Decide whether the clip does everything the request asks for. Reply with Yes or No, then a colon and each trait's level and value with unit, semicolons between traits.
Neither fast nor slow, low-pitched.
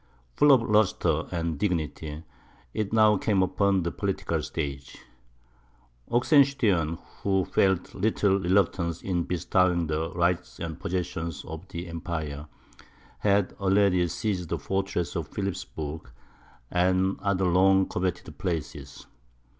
No: slow, 120 wpm; very low, 90 Hz